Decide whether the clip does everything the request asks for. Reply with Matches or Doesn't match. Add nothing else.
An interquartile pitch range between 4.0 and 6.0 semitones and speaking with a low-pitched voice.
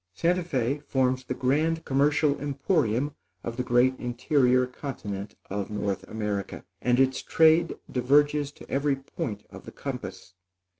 Doesn't match